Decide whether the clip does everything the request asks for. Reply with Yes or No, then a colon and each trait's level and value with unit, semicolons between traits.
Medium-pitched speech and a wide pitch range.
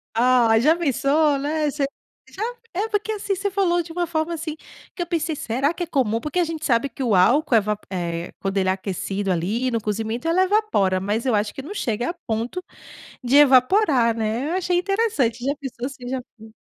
No: very high, 270 Hz; wide, 7.1 semitones